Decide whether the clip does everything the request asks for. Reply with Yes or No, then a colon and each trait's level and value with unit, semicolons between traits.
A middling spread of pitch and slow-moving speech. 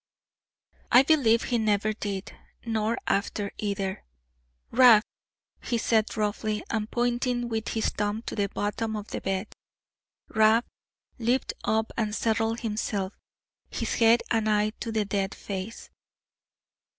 No: narrow, 1.8 semitones; slow, 130 wpm